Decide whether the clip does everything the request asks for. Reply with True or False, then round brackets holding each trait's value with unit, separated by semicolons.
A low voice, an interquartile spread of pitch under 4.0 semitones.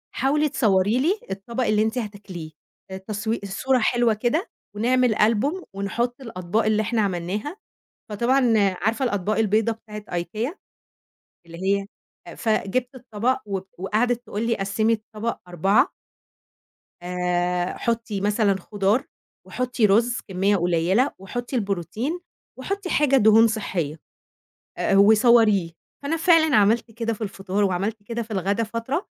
False (215 Hz; 3.5 semitones)